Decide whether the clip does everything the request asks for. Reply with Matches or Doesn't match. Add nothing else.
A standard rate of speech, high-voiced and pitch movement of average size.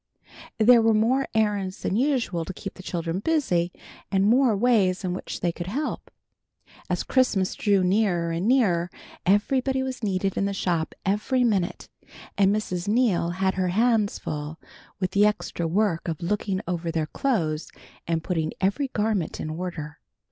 Matches